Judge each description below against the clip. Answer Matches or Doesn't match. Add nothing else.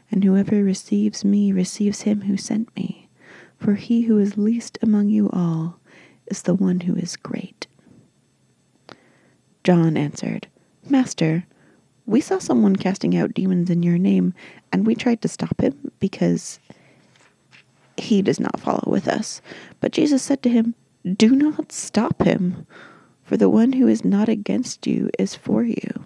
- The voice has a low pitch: Doesn't match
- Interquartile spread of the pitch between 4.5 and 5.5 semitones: Doesn't match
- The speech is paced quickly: Doesn't match